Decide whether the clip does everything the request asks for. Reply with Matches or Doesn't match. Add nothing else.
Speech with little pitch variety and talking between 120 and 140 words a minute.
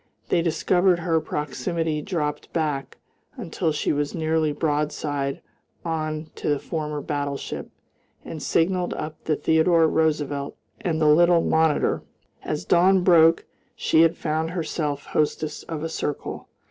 Matches